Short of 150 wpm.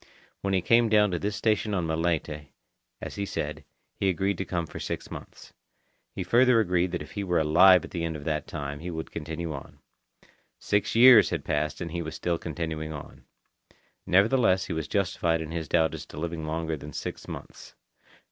No: average, 200 wpm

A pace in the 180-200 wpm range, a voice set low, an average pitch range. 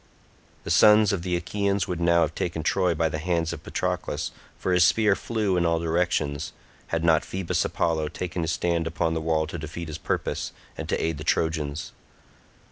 No: average, 195 wpm; very low, 85 Hz; narrow, 2.0 semitones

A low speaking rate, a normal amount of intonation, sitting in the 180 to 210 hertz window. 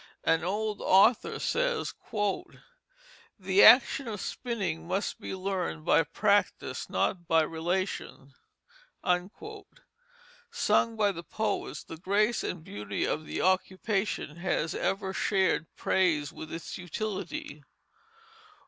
Yes: slow, 110 wpm; average, 4.5 semitones; high, 190 Hz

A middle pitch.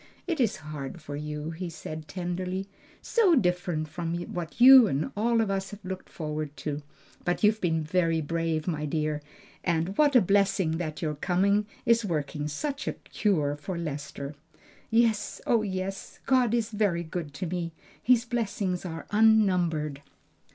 Yes: medium, 180 Hz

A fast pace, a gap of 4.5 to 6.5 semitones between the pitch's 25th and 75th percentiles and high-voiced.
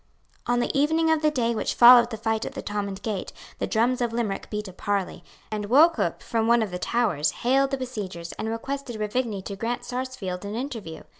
No: fast, 210 wpm; average, 3.8 semitones; high, 230 Hz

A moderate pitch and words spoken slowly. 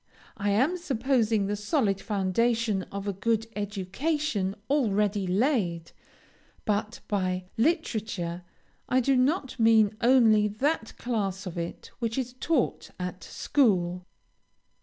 No: high, 215 Hz; slow, 115 wpm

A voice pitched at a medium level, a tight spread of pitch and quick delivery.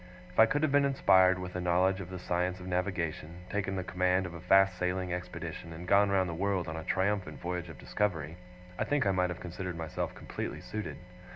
No: very low, 90 Hz; narrow, 1.6 semitones; fast, 220 wpm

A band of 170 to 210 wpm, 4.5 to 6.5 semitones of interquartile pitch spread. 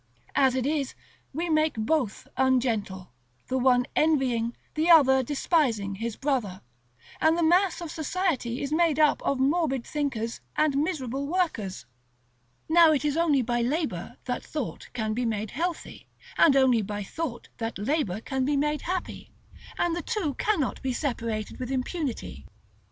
No: average, 155 wpm; average, 4.9 semitones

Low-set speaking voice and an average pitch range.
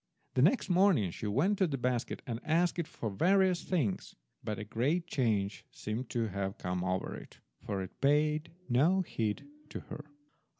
No: low, 125 Hz; wide, 8.3 semitones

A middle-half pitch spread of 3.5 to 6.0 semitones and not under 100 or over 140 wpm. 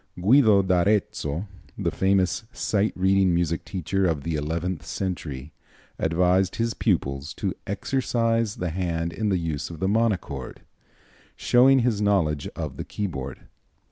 Yes: average, 4.0 semitones; slow, 135 wpm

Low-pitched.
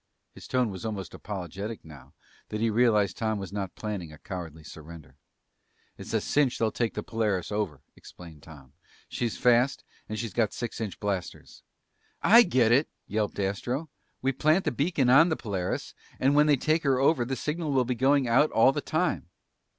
Yes: low, 115 Hz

